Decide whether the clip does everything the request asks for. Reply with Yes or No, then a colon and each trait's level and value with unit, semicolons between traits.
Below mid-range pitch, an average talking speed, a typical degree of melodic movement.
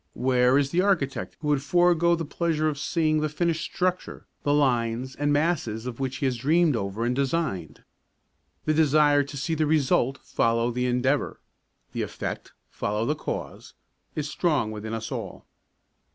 No: medium, 145 Hz; average, 165 wpm; average, 4.0 semitones